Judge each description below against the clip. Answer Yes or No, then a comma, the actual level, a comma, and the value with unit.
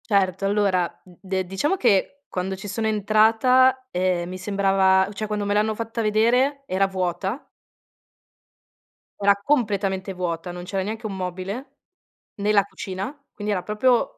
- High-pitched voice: Yes, high, 200 Hz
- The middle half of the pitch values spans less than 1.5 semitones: No, narrow, 2.6 semitones